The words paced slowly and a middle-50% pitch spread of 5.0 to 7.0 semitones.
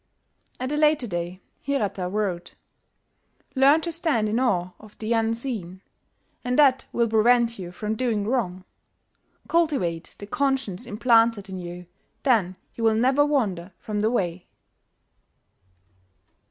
Yes: slow, 130 wpm; wide, 5.5 semitones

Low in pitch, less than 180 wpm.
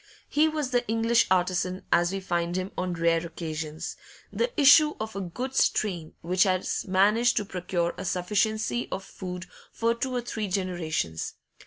No: high, 190 Hz; average, 165 wpm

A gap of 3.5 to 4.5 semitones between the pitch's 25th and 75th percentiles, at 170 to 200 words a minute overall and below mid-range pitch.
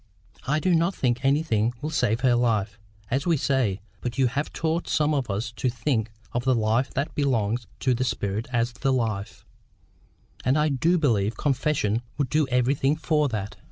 Yes: average, 4.0 semitones; average, 185 wpm; low, 125 Hz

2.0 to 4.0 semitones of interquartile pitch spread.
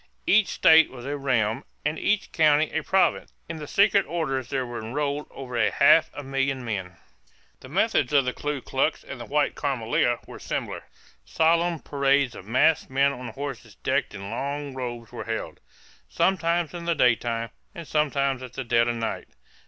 No: average, 4.4 semitones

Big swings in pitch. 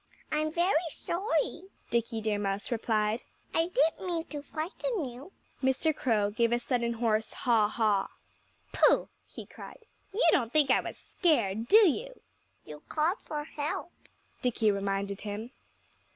Yes: wide, 6.8 semitones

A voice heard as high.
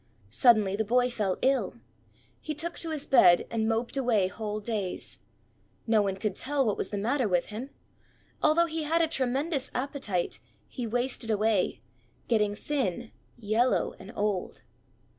Yes: high, 230 Hz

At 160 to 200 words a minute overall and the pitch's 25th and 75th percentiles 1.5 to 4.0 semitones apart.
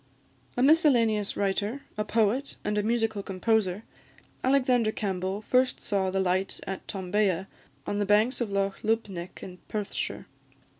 No: average, 140 wpm; average, 3.0 semitones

